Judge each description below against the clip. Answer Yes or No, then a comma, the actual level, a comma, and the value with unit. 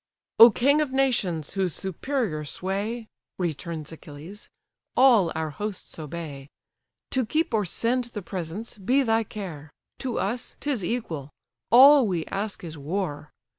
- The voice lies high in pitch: Yes, high, 200 Hz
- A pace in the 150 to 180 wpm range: No, slow, 135 wpm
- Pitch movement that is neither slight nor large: No, wide, 6.7 semitones